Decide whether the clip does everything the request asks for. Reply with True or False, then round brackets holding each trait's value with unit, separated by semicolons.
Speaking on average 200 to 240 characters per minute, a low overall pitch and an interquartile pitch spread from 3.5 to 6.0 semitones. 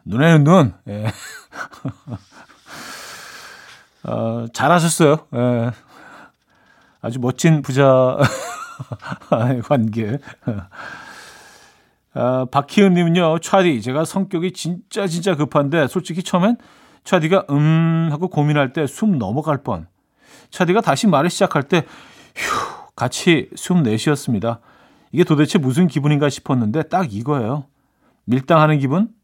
False (215 characters per minute; 150 Hz; 5.5 semitones)